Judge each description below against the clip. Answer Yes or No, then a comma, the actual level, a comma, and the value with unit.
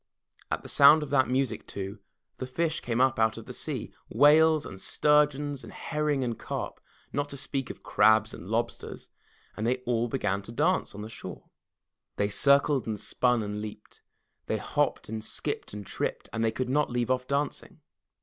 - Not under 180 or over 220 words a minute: Yes, average, 190 wpm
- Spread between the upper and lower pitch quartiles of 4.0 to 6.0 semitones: Yes, average, 4.6 semitones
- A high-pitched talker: No, low, 125 Hz